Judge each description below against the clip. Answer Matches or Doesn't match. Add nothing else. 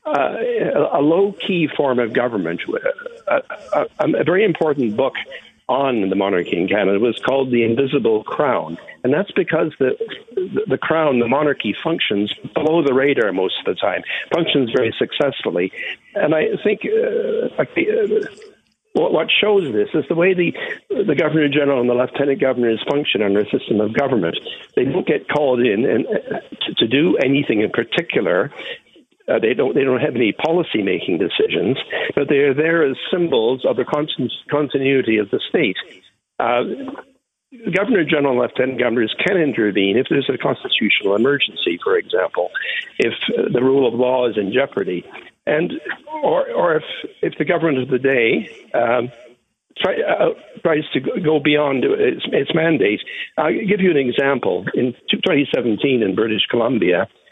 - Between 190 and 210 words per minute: Doesn't match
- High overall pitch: Matches